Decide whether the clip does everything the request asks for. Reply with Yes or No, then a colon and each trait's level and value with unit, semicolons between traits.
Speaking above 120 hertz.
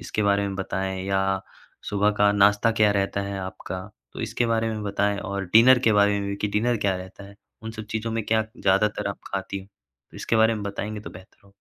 No: low, 100 Hz